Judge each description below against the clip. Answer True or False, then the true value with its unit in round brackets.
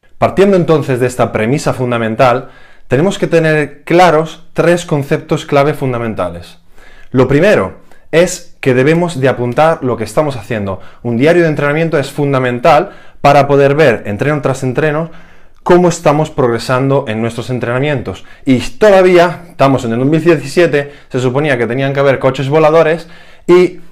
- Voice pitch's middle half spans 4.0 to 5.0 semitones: True (4.3 semitones)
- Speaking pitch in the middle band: True (145 Hz)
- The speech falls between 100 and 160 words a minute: True (145 wpm)